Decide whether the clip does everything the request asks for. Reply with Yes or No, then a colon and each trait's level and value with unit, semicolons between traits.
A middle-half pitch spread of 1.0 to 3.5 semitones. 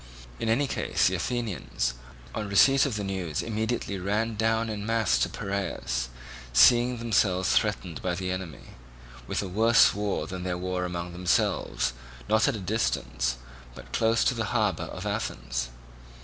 No: average, 4.1 semitones